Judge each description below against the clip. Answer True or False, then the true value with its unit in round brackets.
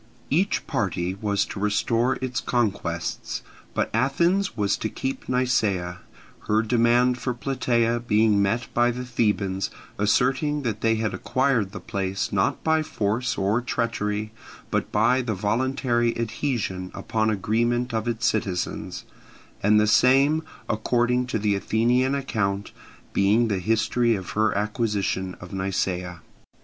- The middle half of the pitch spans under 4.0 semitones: True (3.6 semitones)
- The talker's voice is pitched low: True (110 Hz)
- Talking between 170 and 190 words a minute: False (135 wpm)